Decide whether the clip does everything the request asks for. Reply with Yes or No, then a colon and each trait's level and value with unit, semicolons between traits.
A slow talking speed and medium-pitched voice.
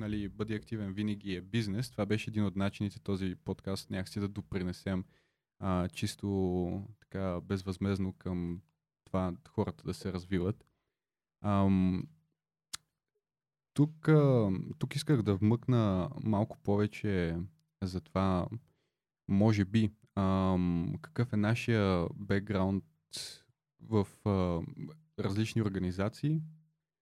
No: slow, 105 wpm; low, 100 Hz